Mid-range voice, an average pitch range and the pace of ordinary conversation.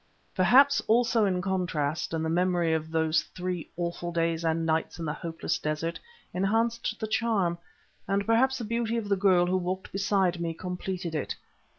Yes: medium, 180 Hz; average, 3.7 semitones; average, 175 wpm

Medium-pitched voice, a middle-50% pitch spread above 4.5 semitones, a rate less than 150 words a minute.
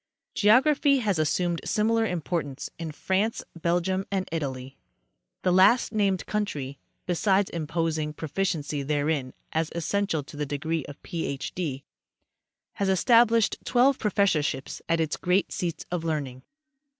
Yes: medium, 170 Hz; average, 4.9 semitones; average, 140 wpm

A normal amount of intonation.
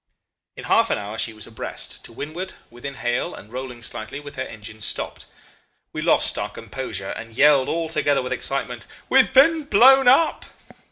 No: wide, 6.6 semitones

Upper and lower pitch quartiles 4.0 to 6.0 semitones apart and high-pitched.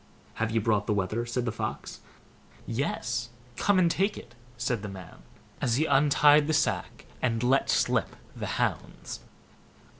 No: average, 4.5 semitones; low, 120 Hz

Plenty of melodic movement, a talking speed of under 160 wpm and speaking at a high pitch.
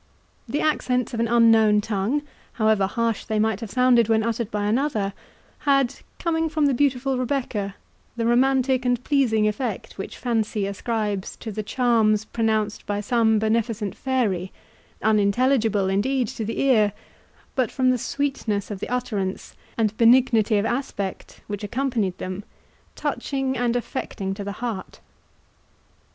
No: average, 3.4 semitones; average, 140 wpm; high, 225 Hz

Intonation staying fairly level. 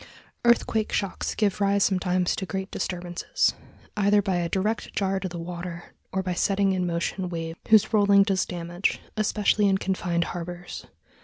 Yes: narrow, 2.3 semitones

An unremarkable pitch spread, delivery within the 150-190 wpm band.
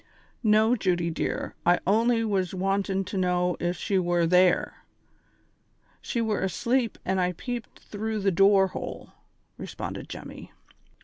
No: average, 3.3 semitones; slow, 135 wpm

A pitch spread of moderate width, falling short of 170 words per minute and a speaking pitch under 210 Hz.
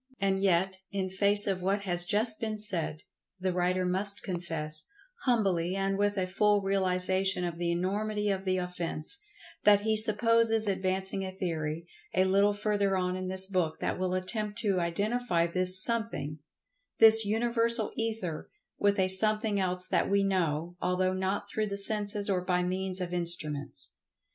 No: narrow, 2.3 semitones; average, 160 wpm; high, 190 Hz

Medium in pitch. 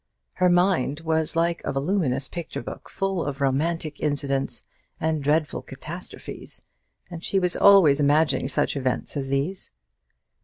Yes: medium, 155 Hz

